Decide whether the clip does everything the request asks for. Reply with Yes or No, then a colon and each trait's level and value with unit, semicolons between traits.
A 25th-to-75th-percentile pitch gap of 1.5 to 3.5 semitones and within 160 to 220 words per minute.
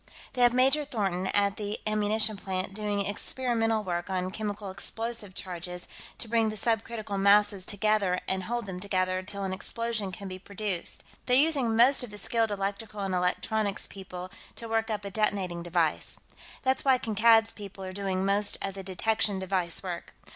Yes: average, 2.9 semitones; average, 175 wpm